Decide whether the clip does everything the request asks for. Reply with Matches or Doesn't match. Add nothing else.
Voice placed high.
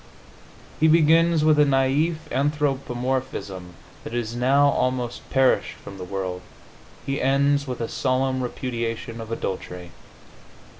Doesn't match